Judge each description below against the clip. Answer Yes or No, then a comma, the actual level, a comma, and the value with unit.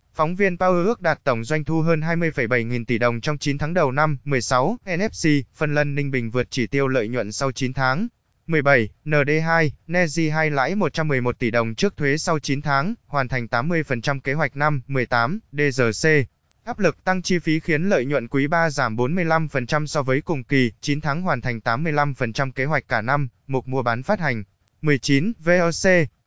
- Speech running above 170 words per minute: Yes, average, 195 wpm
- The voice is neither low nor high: Yes, medium, 145 Hz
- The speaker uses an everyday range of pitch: Yes, average, 4.0 semitones